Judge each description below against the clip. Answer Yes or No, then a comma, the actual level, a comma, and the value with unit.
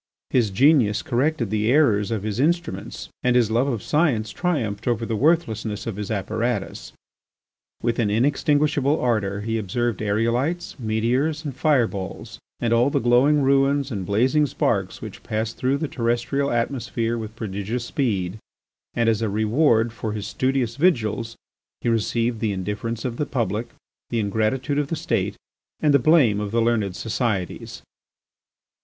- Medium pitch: No, low, 115 Hz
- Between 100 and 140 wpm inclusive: No, average, 155 wpm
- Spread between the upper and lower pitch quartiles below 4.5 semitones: Yes, average, 4.1 semitones